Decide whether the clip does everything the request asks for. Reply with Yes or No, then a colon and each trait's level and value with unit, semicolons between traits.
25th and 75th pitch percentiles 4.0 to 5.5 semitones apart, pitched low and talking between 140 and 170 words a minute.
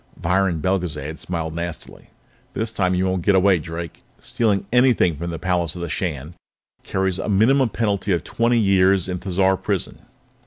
No: narrow, 2.6 semitones; very low, 95 Hz; average, 165 wpm